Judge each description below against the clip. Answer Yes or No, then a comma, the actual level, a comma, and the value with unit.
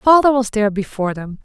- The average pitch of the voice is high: Yes, high, 225 Hz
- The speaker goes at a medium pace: No, fast, 210 wpm